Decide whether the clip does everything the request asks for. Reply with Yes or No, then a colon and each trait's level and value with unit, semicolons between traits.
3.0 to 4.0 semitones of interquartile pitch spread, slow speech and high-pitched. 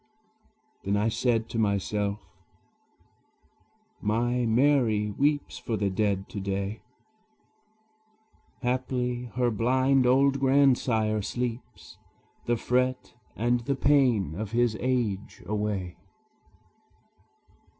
No: average, 3.3 semitones; slow, 95 wpm; low, 120 Hz